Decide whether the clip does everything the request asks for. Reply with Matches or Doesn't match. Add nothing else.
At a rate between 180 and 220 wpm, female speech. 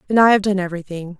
Doesn't match